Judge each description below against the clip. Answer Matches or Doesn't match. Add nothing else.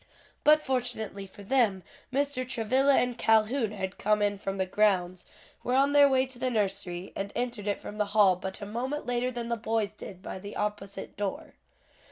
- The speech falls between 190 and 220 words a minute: Matches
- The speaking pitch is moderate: Doesn't match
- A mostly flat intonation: Doesn't match